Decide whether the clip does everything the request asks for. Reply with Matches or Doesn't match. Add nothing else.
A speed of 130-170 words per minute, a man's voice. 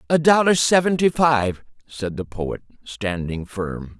Matches